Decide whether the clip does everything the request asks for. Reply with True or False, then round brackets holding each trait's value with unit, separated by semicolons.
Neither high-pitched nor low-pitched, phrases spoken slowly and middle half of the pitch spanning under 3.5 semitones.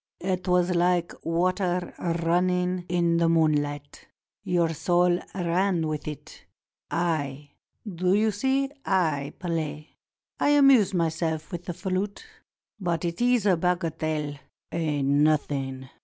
True (170 Hz; 120 wpm; 2.7 semitones)